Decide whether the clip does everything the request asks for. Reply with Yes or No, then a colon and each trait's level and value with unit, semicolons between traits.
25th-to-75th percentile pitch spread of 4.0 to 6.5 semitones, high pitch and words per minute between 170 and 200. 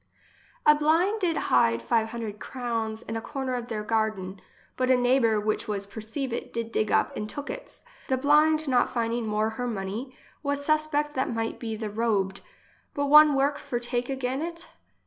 Yes: average, 4.7 semitones; high, 240 Hz; average, 185 wpm